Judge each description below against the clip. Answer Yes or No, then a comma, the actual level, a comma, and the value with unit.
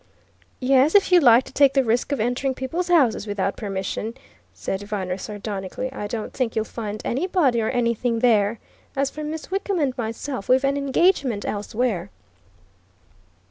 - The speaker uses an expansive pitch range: No, average, 4.6 semitones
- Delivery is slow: No, average, 160 wpm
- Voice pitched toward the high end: Yes, high, 245 Hz